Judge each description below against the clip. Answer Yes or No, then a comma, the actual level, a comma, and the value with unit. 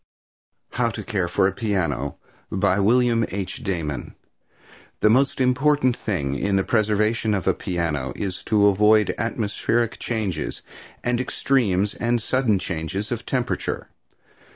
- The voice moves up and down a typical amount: Yes, average, 4.0 semitones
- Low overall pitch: Yes, low, 105 Hz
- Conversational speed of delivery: No, slow, 130 wpm